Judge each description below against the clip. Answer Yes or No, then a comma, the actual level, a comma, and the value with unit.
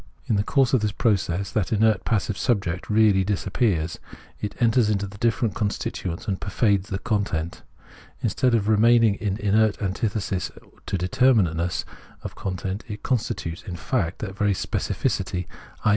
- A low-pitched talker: Yes, low, 100 Hz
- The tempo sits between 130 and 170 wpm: Yes, average, 155 wpm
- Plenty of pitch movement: No, average, 2.8 semitones